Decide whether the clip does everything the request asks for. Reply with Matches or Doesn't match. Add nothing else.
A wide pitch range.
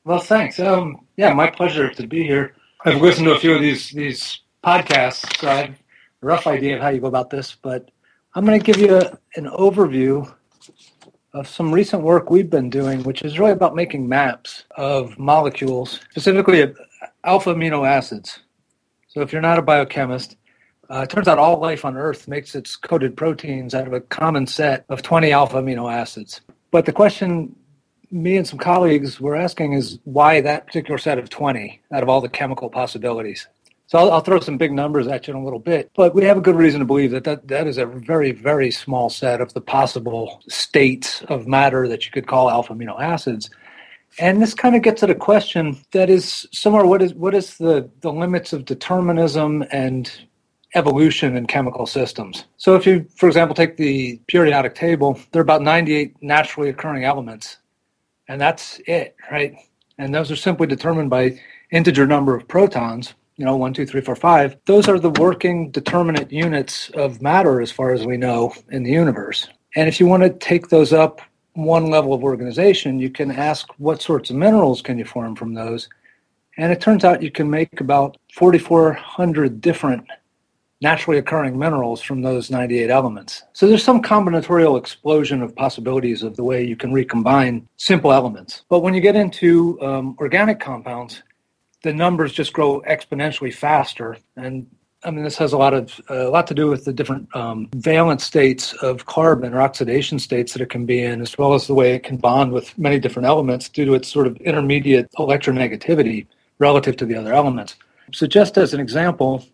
Doesn't match